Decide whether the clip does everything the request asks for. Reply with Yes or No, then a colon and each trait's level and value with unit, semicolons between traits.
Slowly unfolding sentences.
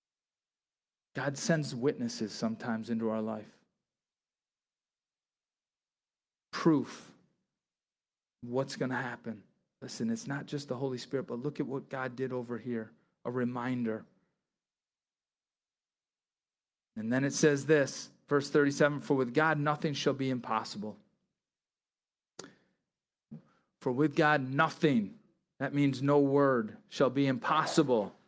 Yes: slow, 115 wpm